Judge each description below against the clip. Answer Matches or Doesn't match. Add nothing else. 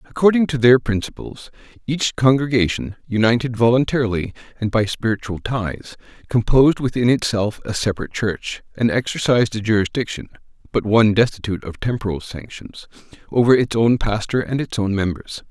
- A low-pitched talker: Matches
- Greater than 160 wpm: Doesn't match